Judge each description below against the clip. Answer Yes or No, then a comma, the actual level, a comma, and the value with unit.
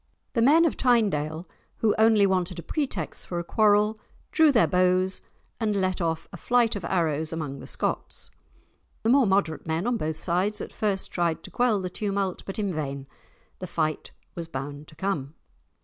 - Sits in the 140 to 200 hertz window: Yes, medium, 185 Hz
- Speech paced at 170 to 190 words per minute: Yes, average, 180 wpm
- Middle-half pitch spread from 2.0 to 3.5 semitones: No, average, 4.8 semitones